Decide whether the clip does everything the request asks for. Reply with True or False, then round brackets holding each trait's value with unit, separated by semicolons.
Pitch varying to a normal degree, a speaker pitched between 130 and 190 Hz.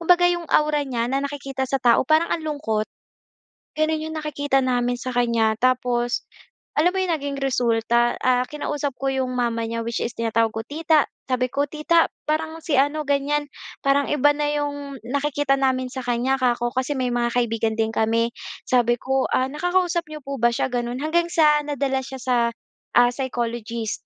False (3.6 semitones; 265 Hz)